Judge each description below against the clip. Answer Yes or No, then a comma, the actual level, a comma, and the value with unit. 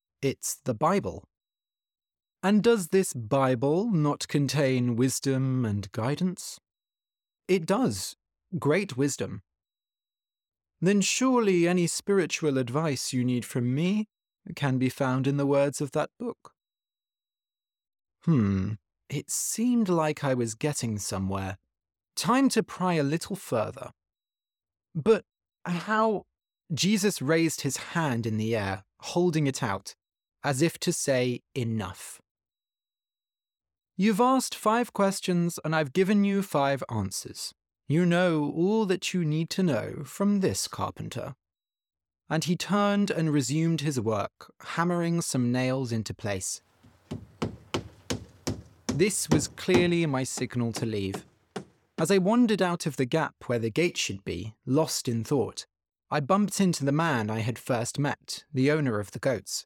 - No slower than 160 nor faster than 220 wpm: No, slow, 135 wpm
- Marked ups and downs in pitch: Yes, wide, 8.0 semitones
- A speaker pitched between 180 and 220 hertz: No, medium, 140 Hz